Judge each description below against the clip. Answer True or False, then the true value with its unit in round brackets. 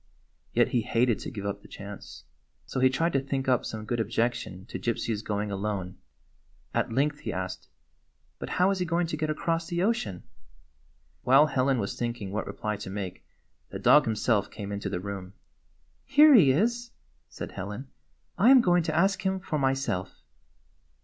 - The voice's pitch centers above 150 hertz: False (120 Hz)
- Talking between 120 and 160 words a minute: False (185 wpm)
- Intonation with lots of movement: True (8.2 semitones)